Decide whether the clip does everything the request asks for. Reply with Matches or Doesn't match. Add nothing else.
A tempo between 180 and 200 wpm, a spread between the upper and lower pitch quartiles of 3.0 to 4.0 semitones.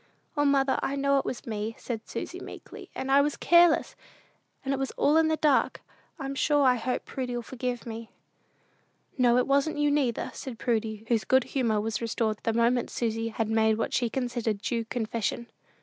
Matches